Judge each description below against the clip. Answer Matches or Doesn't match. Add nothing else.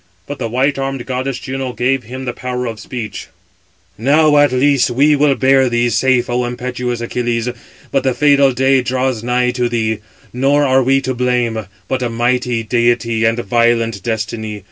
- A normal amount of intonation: Doesn't match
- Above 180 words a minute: Doesn't match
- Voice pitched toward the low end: Matches